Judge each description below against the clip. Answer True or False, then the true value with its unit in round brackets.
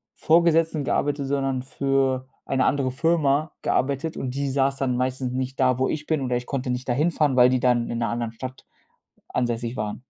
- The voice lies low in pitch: True (130 Hz)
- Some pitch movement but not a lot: False (2.0 semitones)